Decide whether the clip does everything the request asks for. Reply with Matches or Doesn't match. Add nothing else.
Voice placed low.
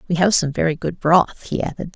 Doesn't match